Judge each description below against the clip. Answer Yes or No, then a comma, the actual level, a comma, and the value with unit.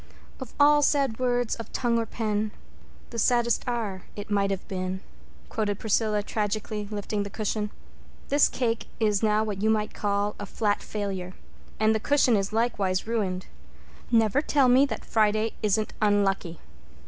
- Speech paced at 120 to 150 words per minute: No, average, 160 wpm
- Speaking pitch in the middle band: No, high, 215 Hz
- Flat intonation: Yes, narrow, 2.3 semitones